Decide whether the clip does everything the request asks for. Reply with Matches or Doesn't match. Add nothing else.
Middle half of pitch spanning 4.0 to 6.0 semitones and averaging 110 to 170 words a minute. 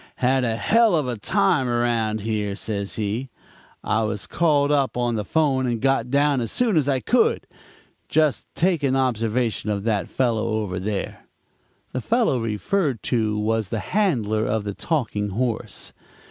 Matches